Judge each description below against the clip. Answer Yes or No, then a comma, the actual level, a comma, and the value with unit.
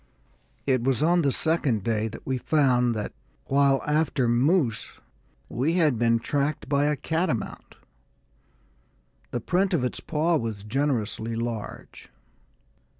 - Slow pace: Yes, slow, 130 wpm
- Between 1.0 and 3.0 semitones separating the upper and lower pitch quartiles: No, average, 4.6 semitones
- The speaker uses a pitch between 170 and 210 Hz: No, low, 135 Hz